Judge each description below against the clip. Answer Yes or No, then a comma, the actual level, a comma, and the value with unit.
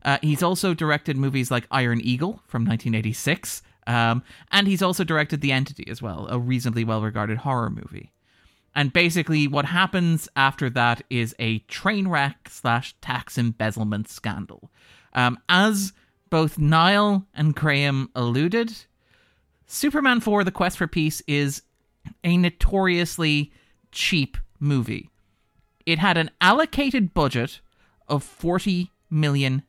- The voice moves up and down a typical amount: No, wide, 6.7 semitones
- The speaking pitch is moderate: Yes, medium, 145 Hz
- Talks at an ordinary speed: No, slow, 130 wpm